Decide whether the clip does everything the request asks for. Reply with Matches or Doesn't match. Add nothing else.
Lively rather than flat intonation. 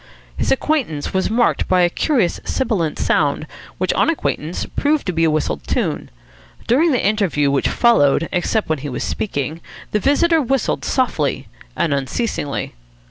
Matches